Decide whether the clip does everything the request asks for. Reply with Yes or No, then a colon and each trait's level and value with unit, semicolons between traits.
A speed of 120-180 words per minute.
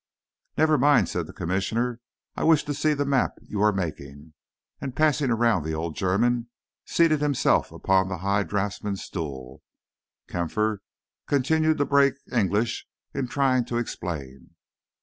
Yes: average, 145 wpm